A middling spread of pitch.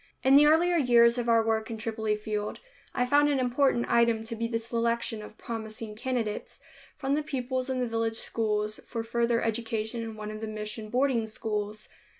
No: narrow, 2.3 semitones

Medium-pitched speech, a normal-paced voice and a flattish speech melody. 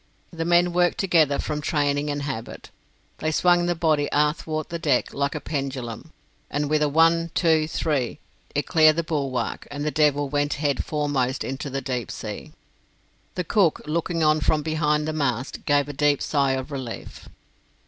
Yes: medium, 150 Hz; average, 175 wpm; narrow, 2.2 semitones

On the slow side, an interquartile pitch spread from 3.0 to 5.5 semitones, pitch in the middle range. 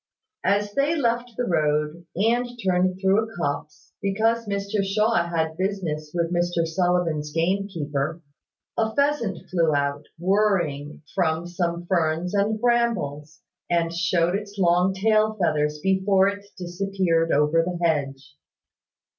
Yes: slow, 130 wpm; average, 3.9 semitones; medium, 180 Hz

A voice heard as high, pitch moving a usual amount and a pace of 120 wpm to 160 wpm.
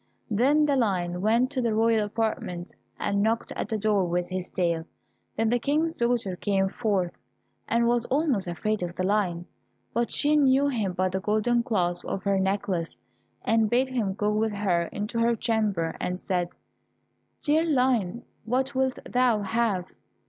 No: high, 215 Hz; average, 4.3 semitones; average, 170 wpm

